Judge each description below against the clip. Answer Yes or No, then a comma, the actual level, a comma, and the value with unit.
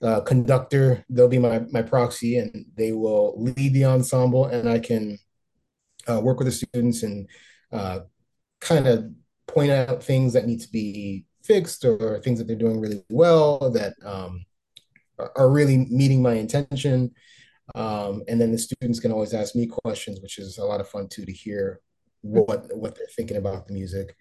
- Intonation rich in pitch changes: No, average, 3.7 semitones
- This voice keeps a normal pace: Yes, average, 180 wpm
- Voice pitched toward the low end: Yes, low, 115 Hz